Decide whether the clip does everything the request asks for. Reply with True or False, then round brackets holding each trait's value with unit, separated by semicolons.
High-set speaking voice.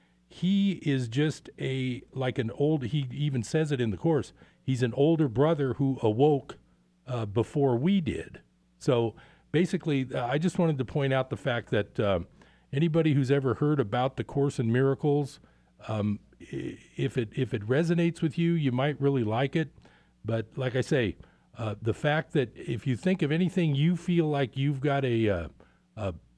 False (135 Hz)